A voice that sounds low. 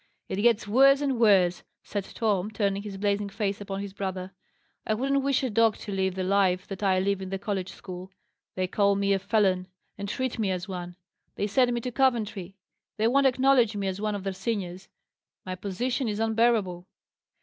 No: high, 200 Hz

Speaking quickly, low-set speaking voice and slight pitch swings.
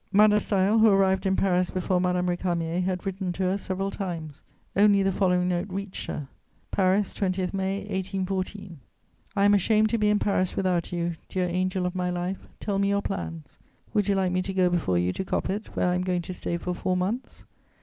No: fast, 210 wpm; medium, 185 Hz; narrow, 1.7 semitones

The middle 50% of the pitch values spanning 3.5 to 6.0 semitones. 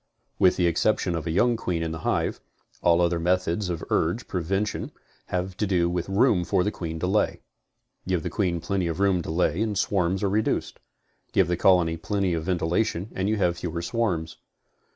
No: narrow, 2.6 semitones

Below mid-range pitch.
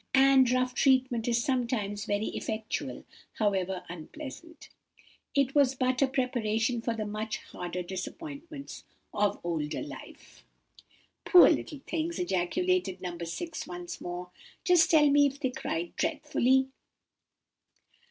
No: very high, 250 Hz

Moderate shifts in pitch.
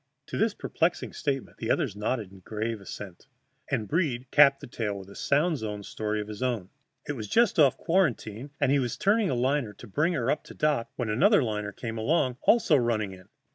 No: wide, 5.8 semitones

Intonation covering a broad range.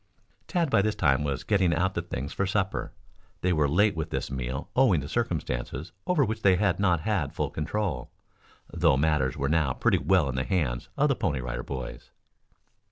Yes: wide, 6.6 semitones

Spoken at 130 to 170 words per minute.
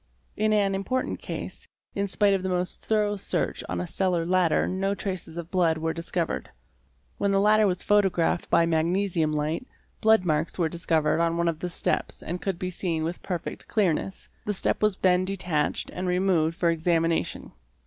No: average, 180 wpm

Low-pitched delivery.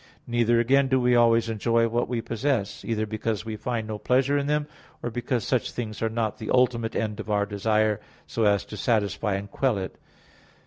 Yes: low, 115 Hz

